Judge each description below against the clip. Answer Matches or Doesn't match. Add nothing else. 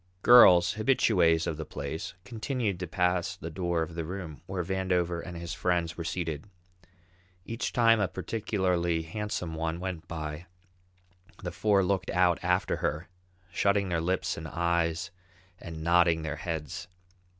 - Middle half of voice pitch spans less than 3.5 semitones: Matches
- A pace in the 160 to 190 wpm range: Doesn't match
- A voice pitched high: Doesn't match